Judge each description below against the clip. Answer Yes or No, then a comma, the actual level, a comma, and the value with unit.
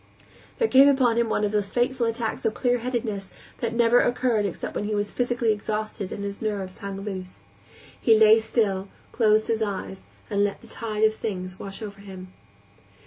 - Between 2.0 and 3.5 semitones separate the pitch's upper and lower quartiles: Yes, average, 2.7 semitones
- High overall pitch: Yes, high, 215 Hz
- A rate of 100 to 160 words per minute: No, average, 185 wpm